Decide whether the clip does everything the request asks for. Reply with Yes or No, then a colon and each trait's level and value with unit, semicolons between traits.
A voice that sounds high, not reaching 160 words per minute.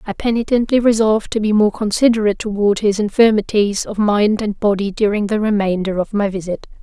No: high, 210 Hz; average, 175 wpm